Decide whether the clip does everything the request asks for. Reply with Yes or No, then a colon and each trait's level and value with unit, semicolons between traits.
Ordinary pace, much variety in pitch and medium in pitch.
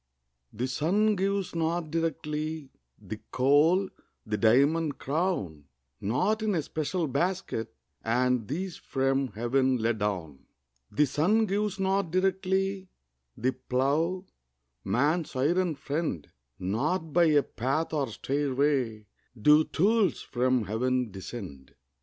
No: slow, 115 wpm; wide, 6.0 semitones; medium, 145 Hz